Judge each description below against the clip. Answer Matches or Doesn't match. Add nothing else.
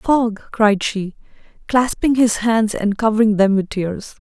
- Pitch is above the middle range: Matches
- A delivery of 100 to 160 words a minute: Matches